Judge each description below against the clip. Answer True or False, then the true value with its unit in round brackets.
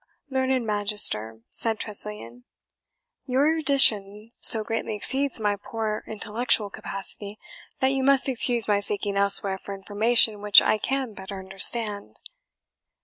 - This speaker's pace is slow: True (125 wpm)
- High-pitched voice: True (210 Hz)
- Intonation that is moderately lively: True (3.2 semitones)